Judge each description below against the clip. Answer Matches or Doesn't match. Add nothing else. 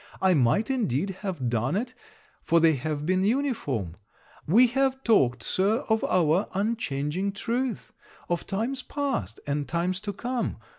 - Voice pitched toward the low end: Doesn't match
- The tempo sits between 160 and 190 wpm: Doesn't match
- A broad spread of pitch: Matches